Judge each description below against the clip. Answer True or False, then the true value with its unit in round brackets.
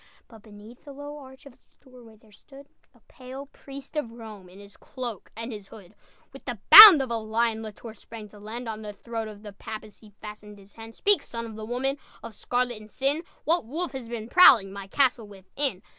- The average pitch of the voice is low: False (230 Hz)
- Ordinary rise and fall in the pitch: True (3.9 semitones)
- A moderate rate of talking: False (220 wpm)